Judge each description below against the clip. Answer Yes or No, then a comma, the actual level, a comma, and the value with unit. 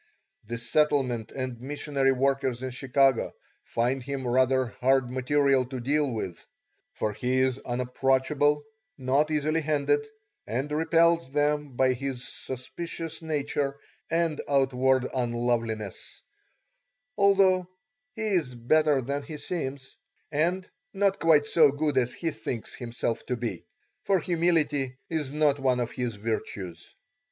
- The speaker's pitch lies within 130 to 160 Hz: Yes, low, 135 Hz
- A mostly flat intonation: No, average, 3.4 semitones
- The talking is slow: Yes, slow, 125 wpm